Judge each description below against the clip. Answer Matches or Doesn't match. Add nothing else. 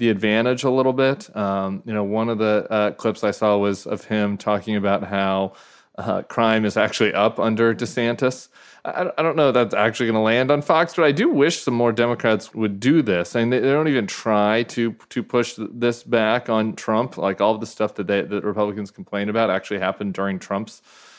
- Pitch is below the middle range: Matches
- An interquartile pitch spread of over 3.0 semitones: Doesn't match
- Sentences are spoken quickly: Matches